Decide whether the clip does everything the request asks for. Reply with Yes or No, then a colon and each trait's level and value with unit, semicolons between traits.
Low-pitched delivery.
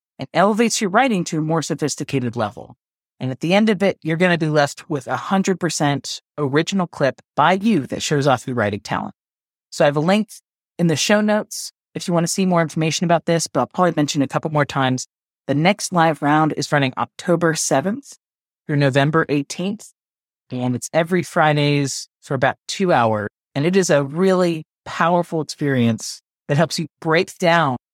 No: medium, 160 Hz